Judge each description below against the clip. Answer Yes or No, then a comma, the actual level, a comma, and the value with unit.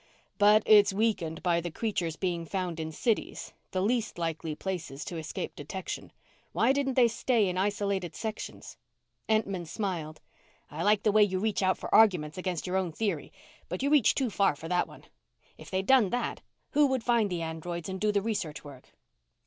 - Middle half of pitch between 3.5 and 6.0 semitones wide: Yes, average, 4.2 semitones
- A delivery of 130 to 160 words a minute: No, average, 190 wpm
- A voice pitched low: No, high, 190 Hz